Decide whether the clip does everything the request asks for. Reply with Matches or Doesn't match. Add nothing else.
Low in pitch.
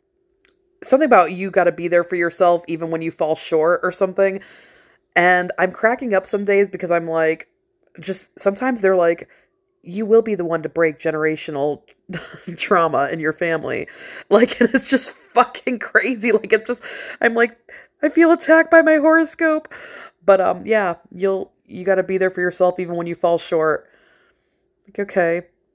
Doesn't match